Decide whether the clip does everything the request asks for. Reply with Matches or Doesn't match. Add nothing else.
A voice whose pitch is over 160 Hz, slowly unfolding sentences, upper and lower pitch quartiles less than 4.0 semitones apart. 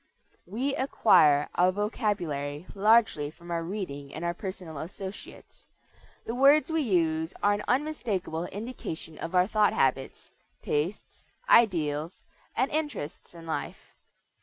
Doesn't match